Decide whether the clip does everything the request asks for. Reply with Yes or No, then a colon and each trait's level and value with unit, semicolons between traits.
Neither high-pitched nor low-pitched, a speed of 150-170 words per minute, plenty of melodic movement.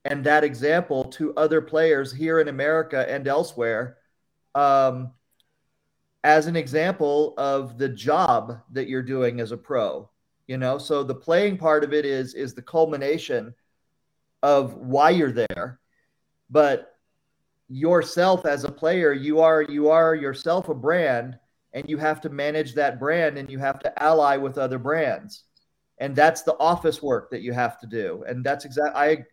No: medium, 145 Hz; average, 165 wpm; average, 3.0 semitones